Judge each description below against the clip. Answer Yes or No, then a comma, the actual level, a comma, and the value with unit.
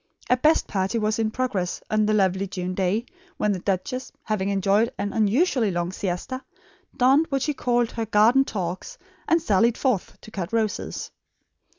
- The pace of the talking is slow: No, average, 170 wpm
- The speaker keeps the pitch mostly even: No, average, 4.5 semitones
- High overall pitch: Yes, high, 215 Hz